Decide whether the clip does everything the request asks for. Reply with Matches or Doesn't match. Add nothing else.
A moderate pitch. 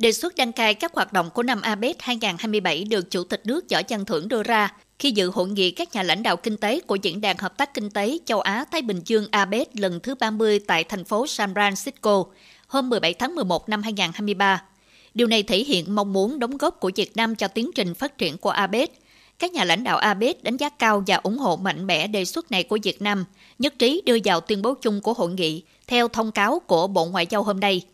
Doesn't match